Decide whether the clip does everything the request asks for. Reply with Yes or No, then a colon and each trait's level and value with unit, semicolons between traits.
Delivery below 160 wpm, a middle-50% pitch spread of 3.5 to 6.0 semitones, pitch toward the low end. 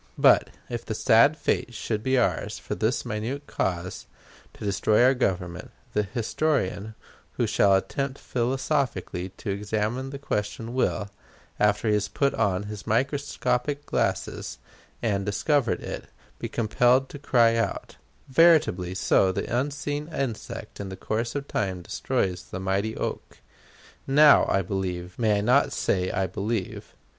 Yes: average, 150 wpm; average, 4.9 semitones; low, 110 Hz